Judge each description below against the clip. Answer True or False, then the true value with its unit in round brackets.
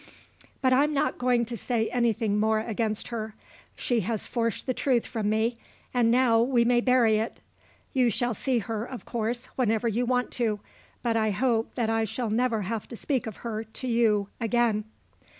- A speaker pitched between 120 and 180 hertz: False (230 Hz)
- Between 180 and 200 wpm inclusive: True (185 wpm)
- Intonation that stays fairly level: True (2.0 semitones)